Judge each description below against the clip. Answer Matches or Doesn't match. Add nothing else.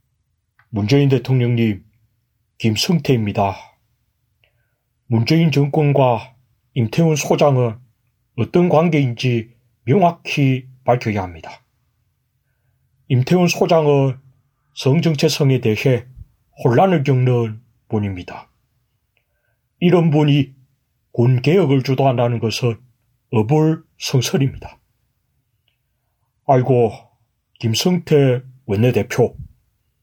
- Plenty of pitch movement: Doesn't match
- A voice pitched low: Matches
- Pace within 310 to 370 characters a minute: Doesn't match